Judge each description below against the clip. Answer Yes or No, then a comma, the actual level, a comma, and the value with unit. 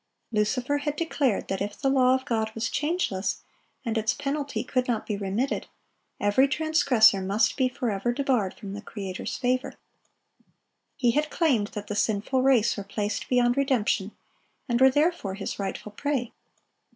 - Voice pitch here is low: No, high, 240 Hz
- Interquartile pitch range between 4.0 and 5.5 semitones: Yes, average, 4.6 semitones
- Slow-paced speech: No, average, 160 wpm